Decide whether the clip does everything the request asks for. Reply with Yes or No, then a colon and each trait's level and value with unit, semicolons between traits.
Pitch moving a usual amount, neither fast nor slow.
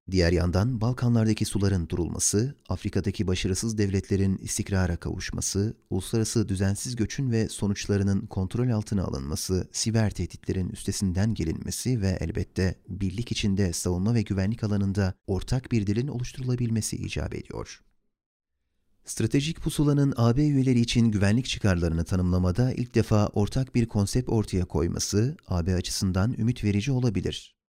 Yes: average, 3.6 semitones; average, 120 wpm